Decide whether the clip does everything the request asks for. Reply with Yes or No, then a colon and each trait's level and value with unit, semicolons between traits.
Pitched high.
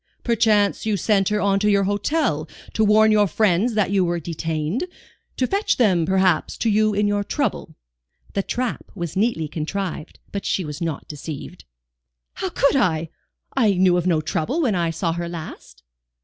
Yes: high, 195 Hz